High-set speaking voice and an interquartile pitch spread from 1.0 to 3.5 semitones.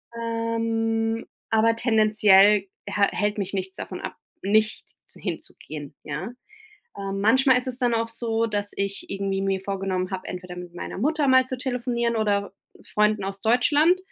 Yes: high, 215 Hz; average, 2.9 semitones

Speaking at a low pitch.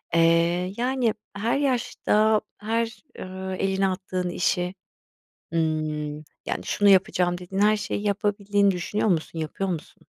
No: high, 190 Hz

